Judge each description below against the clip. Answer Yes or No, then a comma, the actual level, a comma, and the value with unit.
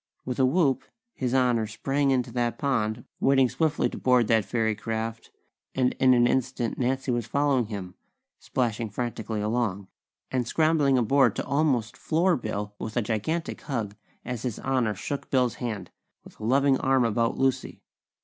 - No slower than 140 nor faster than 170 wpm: Yes, average, 165 wpm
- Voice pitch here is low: Yes, low, 125 Hz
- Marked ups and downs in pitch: No, average, 3.2 semitones